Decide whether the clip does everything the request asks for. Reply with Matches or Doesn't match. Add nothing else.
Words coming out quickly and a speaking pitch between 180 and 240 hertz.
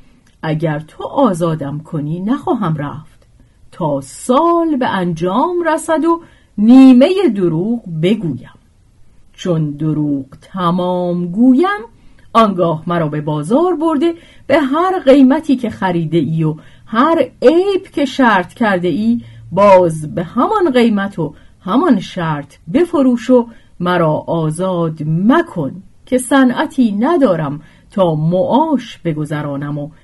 Doesn't match